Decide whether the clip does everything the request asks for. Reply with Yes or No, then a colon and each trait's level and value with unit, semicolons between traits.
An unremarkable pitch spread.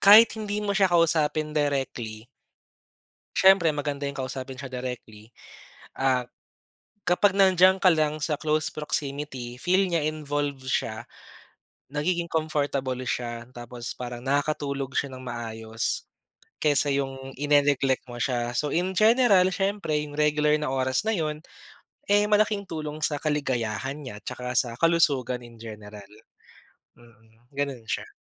Yes: average, 4.1 semitones